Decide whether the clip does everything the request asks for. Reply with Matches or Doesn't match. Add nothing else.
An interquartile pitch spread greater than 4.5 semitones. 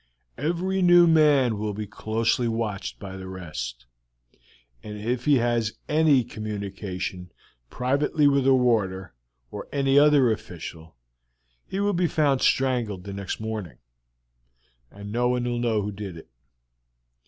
Matches